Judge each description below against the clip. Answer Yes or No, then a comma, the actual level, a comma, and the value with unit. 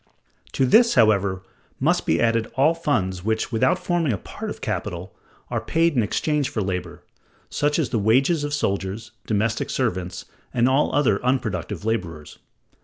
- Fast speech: No, average, 160 wpm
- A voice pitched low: Yes, low, 115 Hz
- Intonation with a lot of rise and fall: Yes, wide, 6.9 semitones